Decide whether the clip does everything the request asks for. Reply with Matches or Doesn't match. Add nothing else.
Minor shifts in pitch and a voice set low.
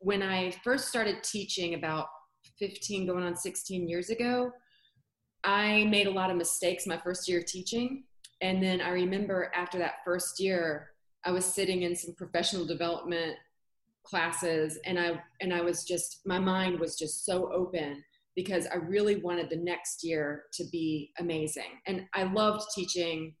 Doesn't match